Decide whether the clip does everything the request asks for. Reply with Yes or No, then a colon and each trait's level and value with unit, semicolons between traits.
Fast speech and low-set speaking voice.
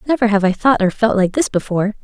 No: fast, 265 wpm; high, 215 Hz